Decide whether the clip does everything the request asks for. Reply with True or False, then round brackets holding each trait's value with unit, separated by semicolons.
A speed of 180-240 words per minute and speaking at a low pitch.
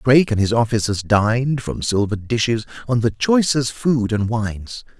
False (170 wpm; 115 Hz)